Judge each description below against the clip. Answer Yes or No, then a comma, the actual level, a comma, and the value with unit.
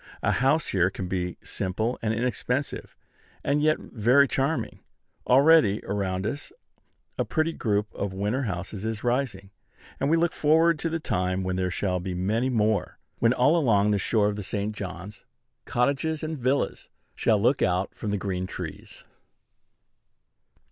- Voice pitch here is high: No, low, 110 Hz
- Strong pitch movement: Yes, wide, 6.3 semitones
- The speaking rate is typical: Yes, average, 160 wpm